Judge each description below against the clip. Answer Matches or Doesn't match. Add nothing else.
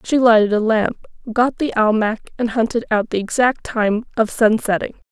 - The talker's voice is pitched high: Matches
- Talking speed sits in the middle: Matches